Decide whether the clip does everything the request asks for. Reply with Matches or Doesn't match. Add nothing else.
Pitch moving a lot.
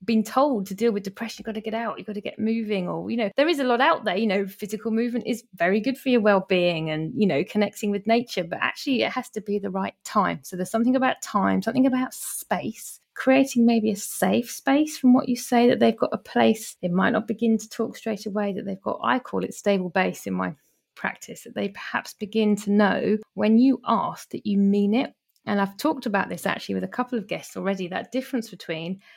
Doesn't match